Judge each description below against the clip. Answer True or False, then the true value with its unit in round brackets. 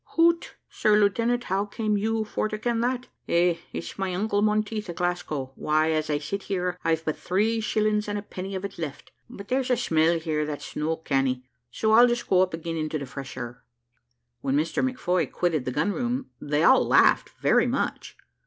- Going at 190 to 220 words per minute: True (200 wpm)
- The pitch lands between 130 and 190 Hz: True (185 Hz)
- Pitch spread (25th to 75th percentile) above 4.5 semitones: True (5.5 semitones)